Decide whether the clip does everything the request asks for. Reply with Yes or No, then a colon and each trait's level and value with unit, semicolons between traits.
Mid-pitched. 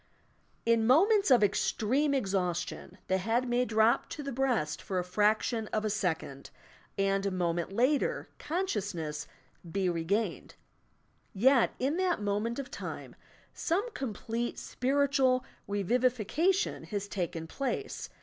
No: high, 220 Hz